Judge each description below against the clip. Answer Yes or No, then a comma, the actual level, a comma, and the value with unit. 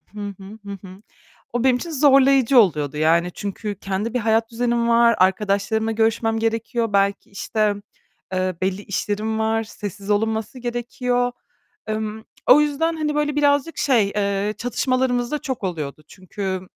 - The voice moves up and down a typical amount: Yes, average, 3.7 semitones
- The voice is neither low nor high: No, high, 220 Hz